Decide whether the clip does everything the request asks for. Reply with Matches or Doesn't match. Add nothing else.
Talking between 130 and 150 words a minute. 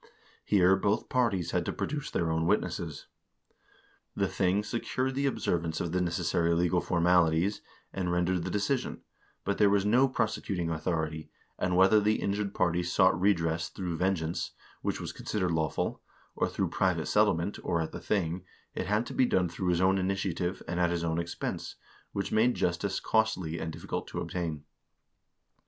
Doesn't match